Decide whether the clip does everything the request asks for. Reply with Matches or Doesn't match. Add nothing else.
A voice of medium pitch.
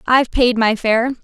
Doesn't match